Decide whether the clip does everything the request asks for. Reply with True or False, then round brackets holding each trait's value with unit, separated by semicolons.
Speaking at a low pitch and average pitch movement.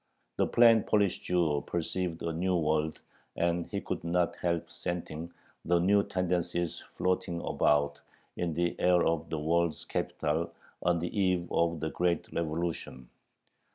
False (85 Hz; 1.5 semitones)